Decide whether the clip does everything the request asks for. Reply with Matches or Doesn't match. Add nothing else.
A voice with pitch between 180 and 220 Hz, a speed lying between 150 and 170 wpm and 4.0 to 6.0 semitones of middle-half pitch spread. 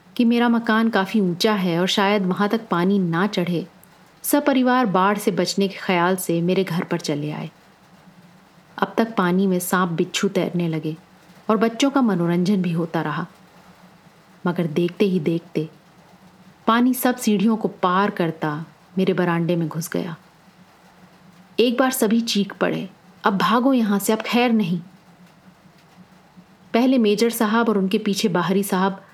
Doesn't match